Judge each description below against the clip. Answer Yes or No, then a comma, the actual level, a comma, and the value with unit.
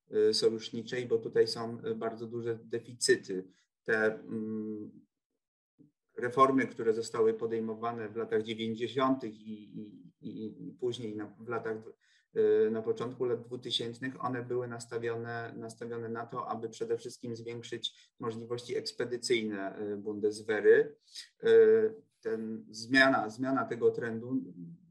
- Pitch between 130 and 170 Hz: No, low, 120 Hz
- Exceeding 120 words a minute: No, slow, 110 wpm